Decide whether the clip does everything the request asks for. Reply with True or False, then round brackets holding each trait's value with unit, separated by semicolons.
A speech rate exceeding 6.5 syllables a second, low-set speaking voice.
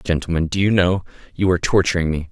True (6.8 syllables/s; 90 Hz)